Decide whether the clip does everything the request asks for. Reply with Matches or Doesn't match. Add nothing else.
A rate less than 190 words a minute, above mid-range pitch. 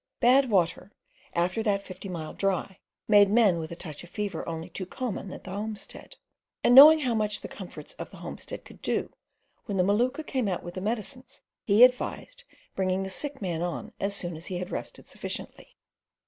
Doesn't match